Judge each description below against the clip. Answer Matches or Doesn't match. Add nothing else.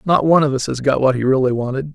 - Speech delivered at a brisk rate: Matches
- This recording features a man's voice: Matches